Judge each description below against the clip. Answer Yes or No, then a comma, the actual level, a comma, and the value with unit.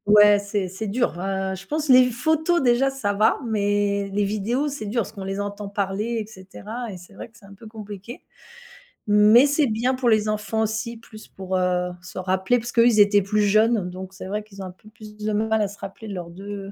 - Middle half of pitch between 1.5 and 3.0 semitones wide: Yes, narrow, 2.6 semitones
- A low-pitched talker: No, high, 210 Hz